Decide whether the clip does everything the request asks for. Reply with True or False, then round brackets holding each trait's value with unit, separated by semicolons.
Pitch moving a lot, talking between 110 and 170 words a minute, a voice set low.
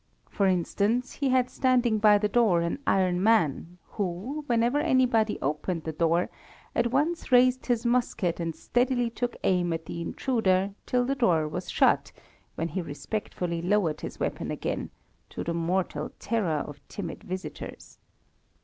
False (6.3 semitones; 155 wpm; 205 Hz)